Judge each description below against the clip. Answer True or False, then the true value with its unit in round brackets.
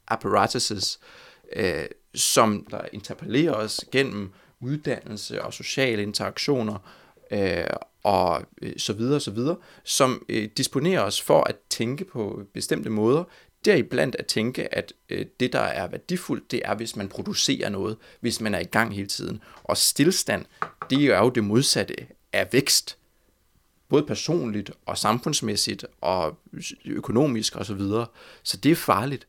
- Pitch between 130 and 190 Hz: False (115 Hz)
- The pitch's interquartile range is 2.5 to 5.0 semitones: False (5.4 semitones)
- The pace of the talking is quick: False (155 wpm)